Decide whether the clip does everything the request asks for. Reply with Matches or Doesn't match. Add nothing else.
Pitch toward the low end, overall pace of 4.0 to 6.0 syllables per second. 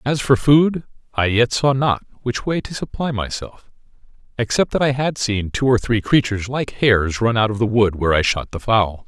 Matches